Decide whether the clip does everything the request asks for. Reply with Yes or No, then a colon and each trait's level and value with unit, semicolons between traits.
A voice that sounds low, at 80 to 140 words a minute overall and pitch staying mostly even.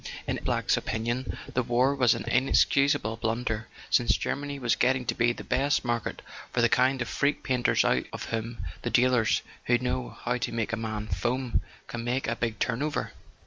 No: low, 120 Hz; average, 200 wpm; narrow, 1.9 semitones